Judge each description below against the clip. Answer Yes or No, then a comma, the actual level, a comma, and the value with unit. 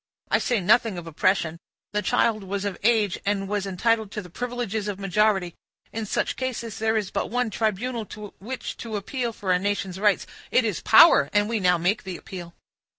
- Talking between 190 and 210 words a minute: Yes, average, 195 wpm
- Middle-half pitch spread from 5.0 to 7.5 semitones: No, average, 3.0 semitones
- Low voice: No, high, 210 Hz